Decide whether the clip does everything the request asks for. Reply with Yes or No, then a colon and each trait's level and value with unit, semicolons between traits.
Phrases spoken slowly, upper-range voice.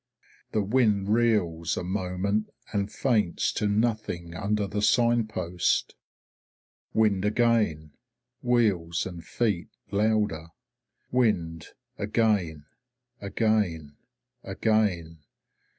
No: slow, 85 wpm; low, 105 Hz